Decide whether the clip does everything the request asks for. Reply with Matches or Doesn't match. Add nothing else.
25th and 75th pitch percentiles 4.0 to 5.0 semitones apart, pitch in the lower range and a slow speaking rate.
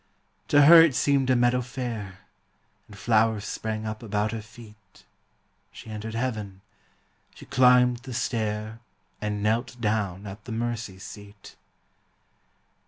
Doesn't match